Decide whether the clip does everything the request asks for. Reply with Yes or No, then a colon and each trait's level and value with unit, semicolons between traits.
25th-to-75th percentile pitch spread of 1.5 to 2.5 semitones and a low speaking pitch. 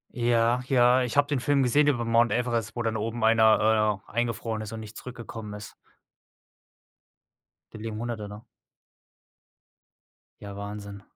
Yes: narrow, 2.1 semitones; low, 115 Hz